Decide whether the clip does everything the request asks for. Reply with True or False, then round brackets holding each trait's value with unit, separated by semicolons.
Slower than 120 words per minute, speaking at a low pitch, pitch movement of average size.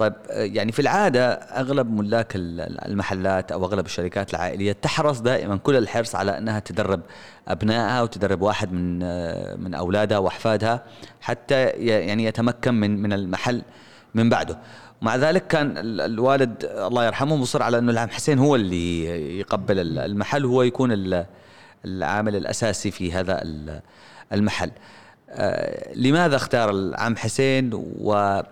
False (125 wpm; 105 Hz; 3.9 semitones)